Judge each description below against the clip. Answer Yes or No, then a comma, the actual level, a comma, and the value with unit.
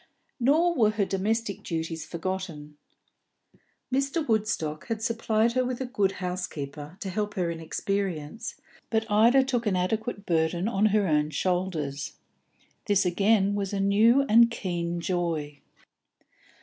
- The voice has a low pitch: No, high, 195 Hz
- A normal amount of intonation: Yes, average, 4.9 semitones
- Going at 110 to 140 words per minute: Yes, slow, 135 wpm